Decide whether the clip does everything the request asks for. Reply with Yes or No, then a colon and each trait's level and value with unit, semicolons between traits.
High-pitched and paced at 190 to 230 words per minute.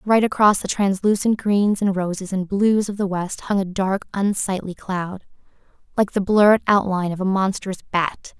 No: high, 195 Hz; average, 180 wpm